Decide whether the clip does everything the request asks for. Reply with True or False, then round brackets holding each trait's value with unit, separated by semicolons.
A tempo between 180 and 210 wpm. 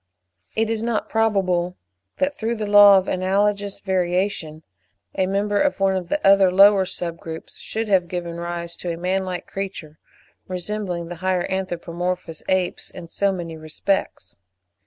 False (155 wpm)